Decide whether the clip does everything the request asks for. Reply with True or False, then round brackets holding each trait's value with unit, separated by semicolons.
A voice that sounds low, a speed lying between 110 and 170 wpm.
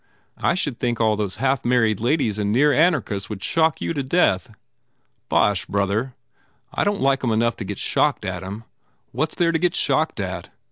False (120 Hz; 200 wpm)